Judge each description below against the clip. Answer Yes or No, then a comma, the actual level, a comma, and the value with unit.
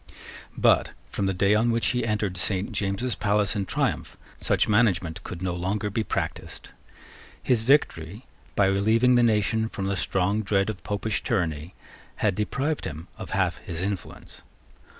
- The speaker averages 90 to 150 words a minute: No, average, 160 wpm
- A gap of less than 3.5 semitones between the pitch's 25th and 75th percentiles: Yes, average, 2.9 semitones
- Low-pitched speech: Yes, low, 100 Hz